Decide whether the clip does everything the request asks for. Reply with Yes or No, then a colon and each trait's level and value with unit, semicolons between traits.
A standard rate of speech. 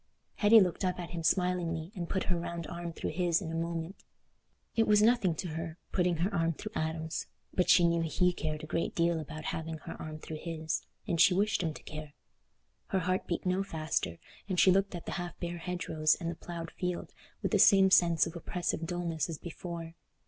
No: fast, 215 wpm